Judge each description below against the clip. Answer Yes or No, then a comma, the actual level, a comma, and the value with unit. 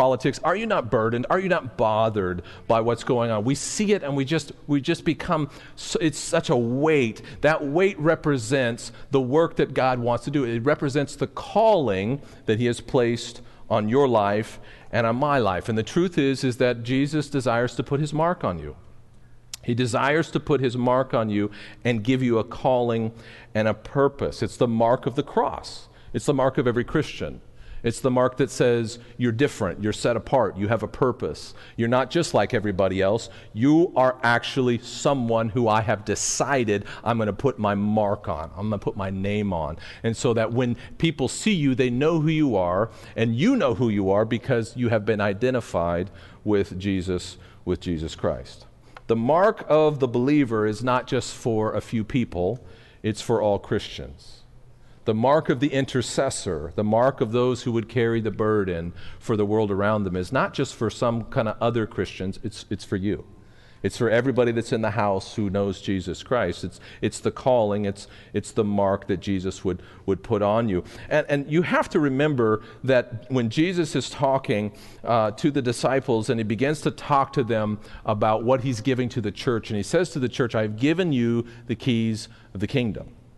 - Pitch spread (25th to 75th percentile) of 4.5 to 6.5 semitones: No, average, 4.1 semitones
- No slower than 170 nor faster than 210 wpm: Yes, average, 200 wpm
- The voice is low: Yes, low, 120 Hz